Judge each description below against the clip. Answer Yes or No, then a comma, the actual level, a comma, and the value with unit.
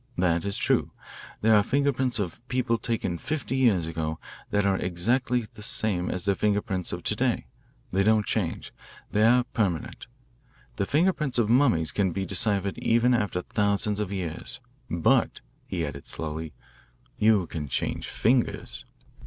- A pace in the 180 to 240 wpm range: No, average, 155 wpm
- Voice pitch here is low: Yes, low, 100 Hz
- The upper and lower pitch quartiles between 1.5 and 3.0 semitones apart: No, average, 4.8 semitones